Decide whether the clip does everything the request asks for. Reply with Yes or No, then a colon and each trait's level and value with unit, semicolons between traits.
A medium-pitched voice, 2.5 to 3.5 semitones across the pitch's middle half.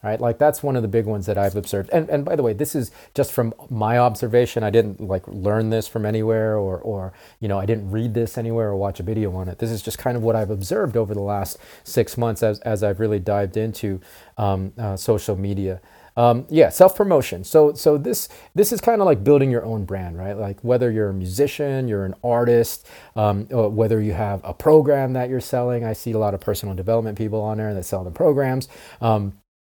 No: low, 110 Hz; average, 3.1 semitones